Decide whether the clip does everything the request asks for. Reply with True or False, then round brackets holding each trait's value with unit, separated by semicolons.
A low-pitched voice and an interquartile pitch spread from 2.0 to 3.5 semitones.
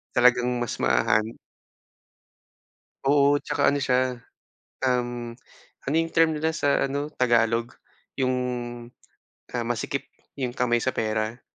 True (125 Hz; 2.9 semitones)